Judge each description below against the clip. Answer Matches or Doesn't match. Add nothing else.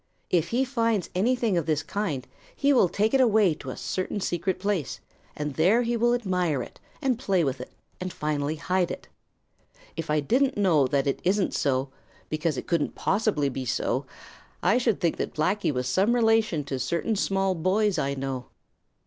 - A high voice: Doesn't match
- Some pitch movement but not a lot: Doesn't match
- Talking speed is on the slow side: Doesn't match